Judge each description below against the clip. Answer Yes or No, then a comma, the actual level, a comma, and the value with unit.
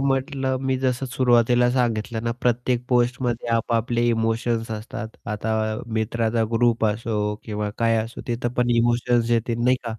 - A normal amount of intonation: No, narrow, 1.4 semitones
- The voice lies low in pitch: Yes, low, 120 Hz